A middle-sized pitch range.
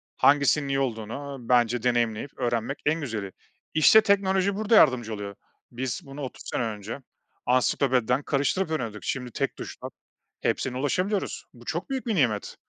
Yes: average, 4.6 semitones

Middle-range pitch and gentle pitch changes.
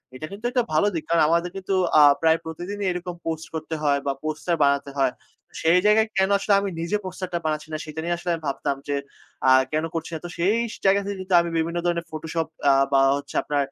No: medium, 170 Hz; average, 3.2 semitones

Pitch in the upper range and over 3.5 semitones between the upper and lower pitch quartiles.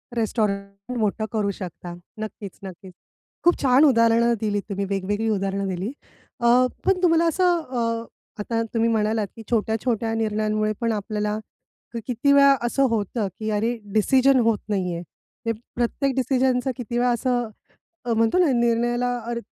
No: high, 230 Hz; average, 2.9 semitones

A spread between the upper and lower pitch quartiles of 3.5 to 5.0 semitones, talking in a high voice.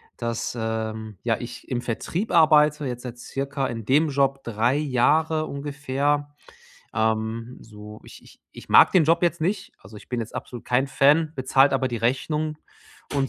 No: average, 4.3 semitones; low, 135 Hz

